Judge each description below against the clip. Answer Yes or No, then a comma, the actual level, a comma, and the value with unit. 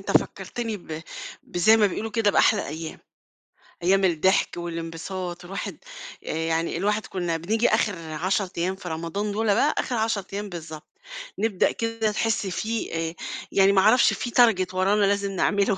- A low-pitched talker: No, high, 195 Hz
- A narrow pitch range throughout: No, average, 3.7 semitones